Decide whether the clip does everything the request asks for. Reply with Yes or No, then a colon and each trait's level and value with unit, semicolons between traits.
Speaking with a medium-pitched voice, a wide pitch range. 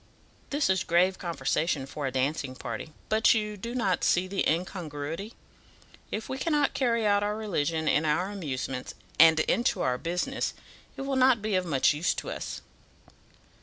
Yes: medium, 180 Hz; wide, 6.2 semitones